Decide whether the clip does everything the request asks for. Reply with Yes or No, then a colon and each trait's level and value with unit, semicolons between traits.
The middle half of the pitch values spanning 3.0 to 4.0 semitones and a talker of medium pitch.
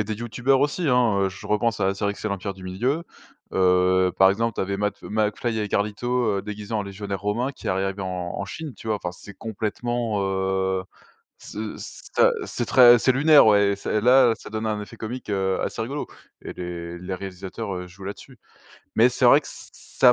No: average, 3.5 semitones; low, 105 Hz